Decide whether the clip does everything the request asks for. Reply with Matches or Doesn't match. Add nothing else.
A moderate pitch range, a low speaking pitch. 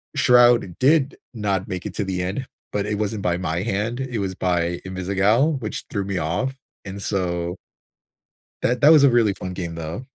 Matches